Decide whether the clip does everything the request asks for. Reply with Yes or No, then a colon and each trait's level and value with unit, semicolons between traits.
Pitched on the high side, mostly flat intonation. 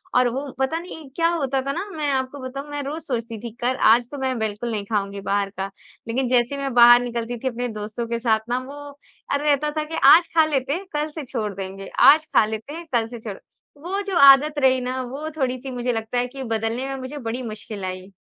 No: very high, 255 Hz; average, 3.8 semitones